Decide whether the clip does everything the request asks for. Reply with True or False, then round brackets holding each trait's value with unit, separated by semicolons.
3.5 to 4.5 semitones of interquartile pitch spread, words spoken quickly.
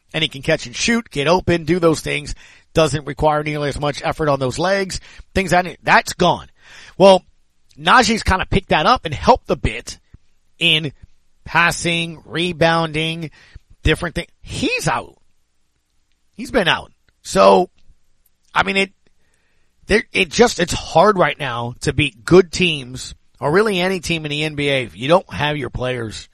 False (4.1 semitones; 165 wpm)